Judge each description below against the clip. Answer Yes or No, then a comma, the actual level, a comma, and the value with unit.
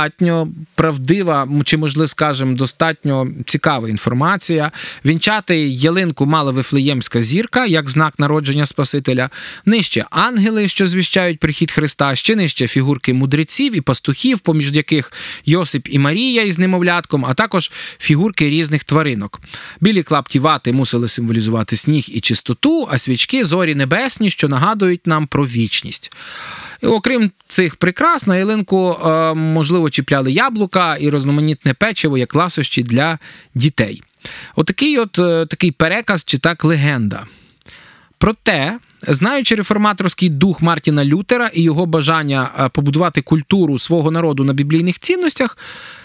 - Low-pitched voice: No, medium, 160 Hz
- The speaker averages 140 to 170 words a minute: No, average, 120 wpm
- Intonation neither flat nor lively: Yes, average, 4.4 semitones